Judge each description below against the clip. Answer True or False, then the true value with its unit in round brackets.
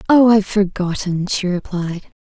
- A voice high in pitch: True (195 Hz)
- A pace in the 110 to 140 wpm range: True (135 wpm)